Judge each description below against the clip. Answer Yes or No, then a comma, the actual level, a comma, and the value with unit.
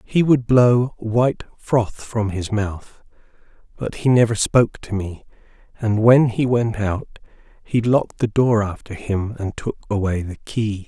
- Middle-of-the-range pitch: No, low, 110 Hz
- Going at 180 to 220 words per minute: No, average, 165 wpm